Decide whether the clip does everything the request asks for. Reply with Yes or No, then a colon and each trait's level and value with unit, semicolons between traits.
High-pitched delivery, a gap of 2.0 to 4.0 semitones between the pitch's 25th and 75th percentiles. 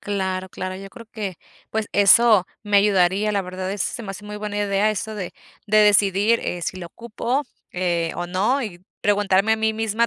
Yes: high, 205 Hz; narrow, 2.5 semitones